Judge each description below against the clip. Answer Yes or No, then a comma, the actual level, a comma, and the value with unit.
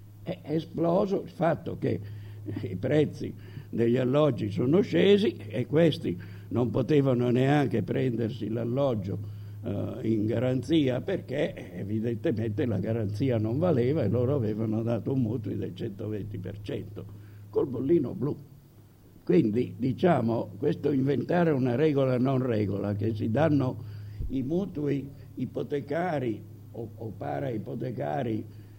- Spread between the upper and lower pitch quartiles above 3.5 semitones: Yes, average, 4.4 semitones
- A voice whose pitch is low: Yes, low, 115 Hz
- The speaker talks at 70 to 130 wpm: Yes, slow, 115 wpm